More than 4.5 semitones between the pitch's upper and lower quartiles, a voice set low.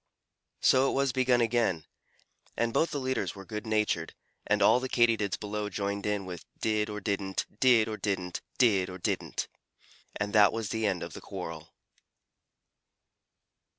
No: average, 3.1 semitones; low, 105 Hz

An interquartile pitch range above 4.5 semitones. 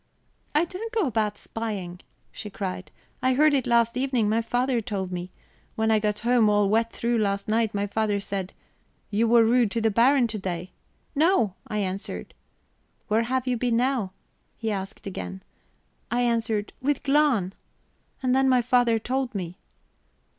No: average, 3.6 semitones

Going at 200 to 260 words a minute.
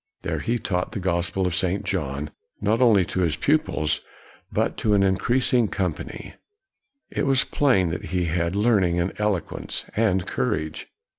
No: average, 155 wpm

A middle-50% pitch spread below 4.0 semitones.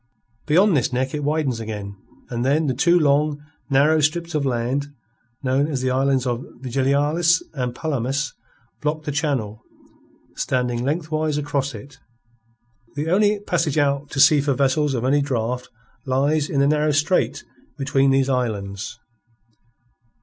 Yes: average, 2.9 semitones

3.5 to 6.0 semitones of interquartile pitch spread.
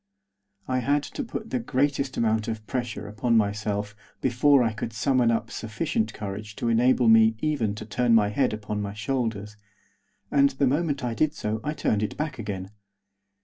Yes: average, 3.9 semitones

